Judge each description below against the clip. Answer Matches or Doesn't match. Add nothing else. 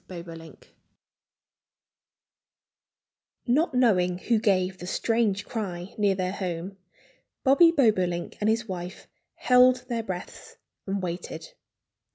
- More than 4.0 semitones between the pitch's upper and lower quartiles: Matches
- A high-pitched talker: Matches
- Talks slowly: Matches